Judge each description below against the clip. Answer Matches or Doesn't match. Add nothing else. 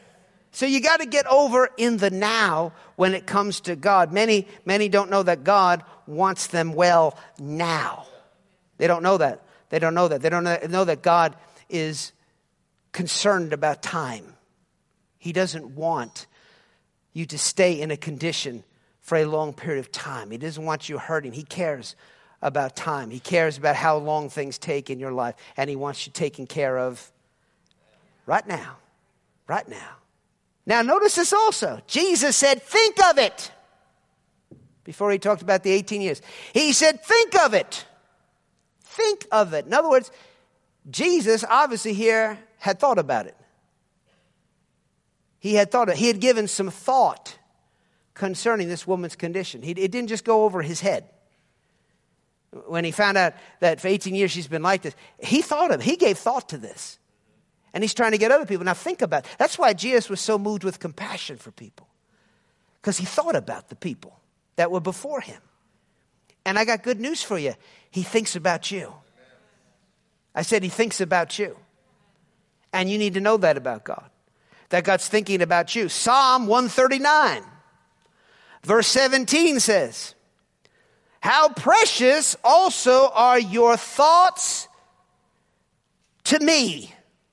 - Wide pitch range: Matches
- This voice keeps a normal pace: Matches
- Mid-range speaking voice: Doesn't match